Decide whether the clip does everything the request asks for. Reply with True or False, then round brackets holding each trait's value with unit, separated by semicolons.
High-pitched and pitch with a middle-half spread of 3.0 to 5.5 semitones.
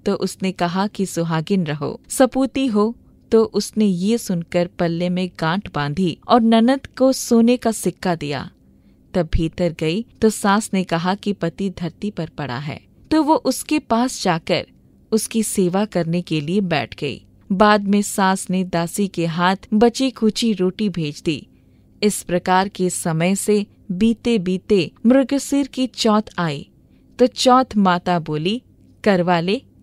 True (195 Hz; 4.3 semitones)